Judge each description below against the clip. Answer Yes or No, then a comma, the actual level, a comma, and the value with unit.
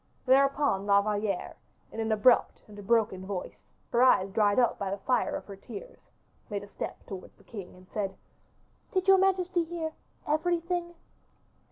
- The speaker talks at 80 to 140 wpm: No, average, 170 wpm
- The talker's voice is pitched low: No, high, 225 Hz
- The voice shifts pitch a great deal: Yes, wide, 8.1 semitones